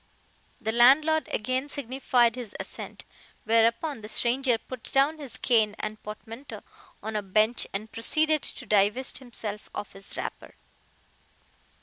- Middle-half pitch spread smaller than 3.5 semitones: No, average, 3.8 semitones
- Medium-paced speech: No, slow, 130 wpm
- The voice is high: Yes, high, 235 Hz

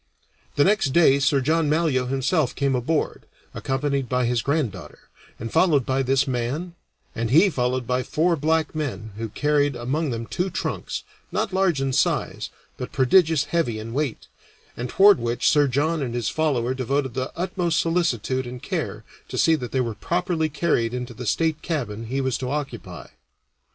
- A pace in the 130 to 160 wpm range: No, average, 175 wpm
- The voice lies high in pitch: No, low, 135 Hz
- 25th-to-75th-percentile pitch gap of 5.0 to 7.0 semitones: No, average, 4.3 semitones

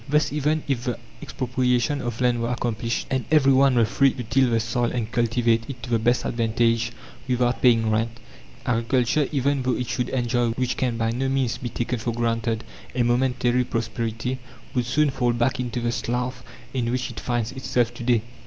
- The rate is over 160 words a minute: Yes, average, 195 wpm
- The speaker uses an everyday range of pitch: No, narrow, 1.7 semitones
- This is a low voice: Yes, low, 120 Hz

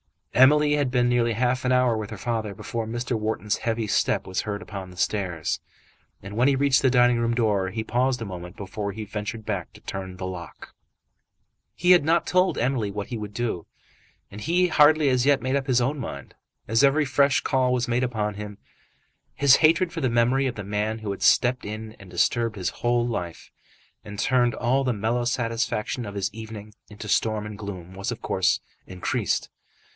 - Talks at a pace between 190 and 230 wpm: Yes, average, 200 wpm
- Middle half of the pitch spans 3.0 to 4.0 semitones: Yes, average, 3.7 semitones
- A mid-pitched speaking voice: No, low, 115 Hz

